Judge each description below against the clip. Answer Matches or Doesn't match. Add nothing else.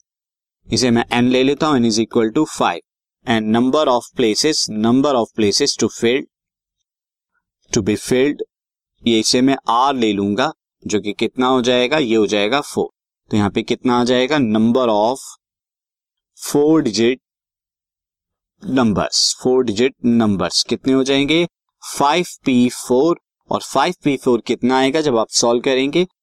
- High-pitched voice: Doesn't match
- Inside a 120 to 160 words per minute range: Matches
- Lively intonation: Doesn't match